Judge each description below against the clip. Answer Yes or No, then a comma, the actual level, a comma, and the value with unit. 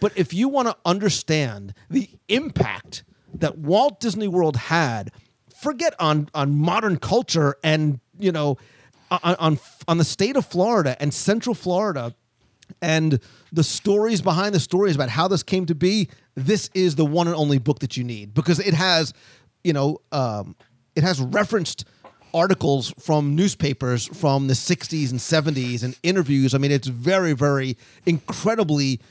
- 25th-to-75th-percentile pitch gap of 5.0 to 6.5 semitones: Yes, wide, 5.6 semitones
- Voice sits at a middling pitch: Yes, medium, 155 Hz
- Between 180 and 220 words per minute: No, average, 160 wpm